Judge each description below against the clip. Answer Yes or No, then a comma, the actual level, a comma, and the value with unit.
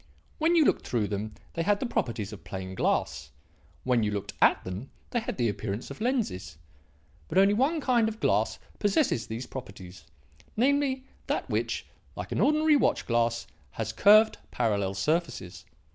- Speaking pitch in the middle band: No, low, 125 Hz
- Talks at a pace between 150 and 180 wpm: Yes, average, 165 wpm